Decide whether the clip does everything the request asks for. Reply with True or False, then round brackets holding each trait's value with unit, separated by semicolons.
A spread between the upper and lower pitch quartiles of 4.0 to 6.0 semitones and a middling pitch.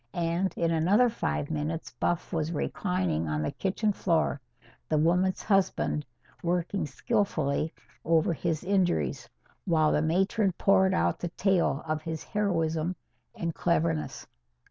False (3.3 semitones; 170 Hz)